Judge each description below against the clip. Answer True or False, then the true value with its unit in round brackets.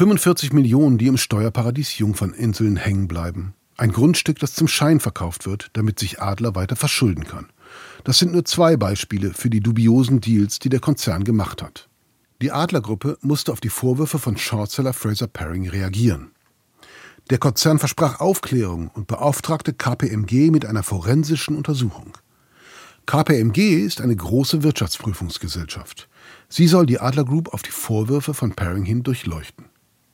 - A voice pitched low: True (120 Hz)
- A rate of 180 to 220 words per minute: False (145 wpm)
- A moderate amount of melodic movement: False (6.2 semitones)